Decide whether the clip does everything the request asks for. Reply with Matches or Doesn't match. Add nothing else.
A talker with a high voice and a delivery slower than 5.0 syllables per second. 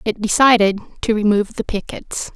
Doesn't match